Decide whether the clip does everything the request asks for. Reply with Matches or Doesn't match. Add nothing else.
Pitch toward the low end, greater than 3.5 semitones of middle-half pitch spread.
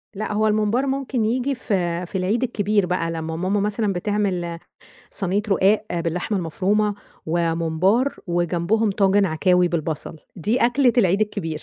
Doesn't match